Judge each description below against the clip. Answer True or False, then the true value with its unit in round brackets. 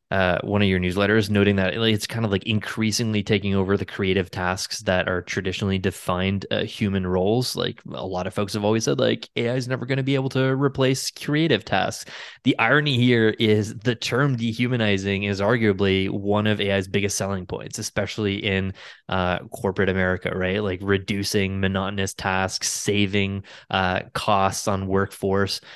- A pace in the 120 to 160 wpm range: False (170 wpm)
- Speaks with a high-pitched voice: False (100 Hz)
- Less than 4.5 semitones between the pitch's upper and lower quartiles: True (2.7 semitones)